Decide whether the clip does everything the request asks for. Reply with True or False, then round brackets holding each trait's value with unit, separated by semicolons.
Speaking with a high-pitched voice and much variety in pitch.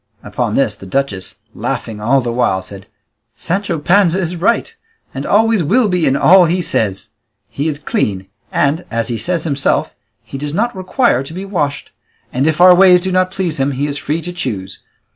False (160 Hz; 5.9 semitones)